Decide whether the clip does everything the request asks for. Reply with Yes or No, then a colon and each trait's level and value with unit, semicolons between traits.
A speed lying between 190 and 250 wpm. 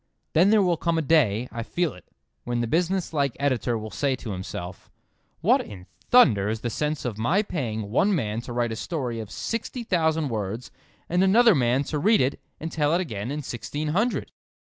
Yes: average, 195 wpm